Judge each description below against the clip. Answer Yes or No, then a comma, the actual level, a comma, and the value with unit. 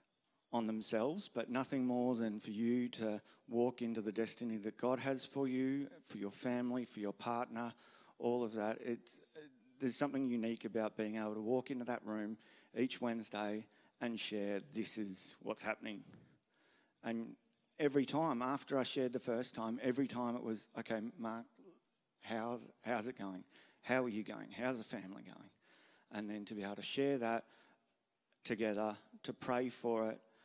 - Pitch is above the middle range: No, low, 115 Hz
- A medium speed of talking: Yes, average, 170 wpm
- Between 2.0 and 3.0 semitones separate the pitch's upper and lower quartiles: Yes, narrow, 2.6 semitones